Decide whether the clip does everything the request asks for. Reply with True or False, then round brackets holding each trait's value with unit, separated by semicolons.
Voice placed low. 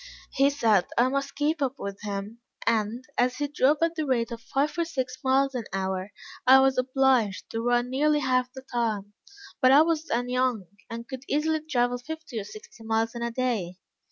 False (255 Hz)